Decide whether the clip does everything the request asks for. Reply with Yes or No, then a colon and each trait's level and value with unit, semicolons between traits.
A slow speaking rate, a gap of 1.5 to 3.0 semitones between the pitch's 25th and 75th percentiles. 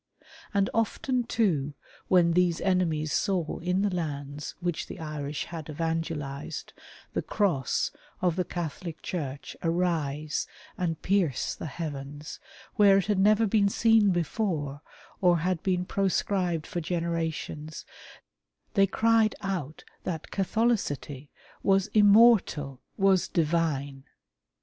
No: slow, 120 wpm; average, 4.4 semitones